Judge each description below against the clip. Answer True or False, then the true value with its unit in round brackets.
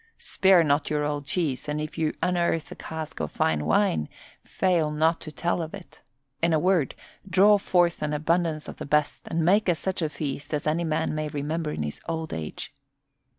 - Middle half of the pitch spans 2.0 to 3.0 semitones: True (2.4 semitones)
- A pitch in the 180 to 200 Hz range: False (155 Hz)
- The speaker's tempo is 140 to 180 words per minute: False (200 wpm)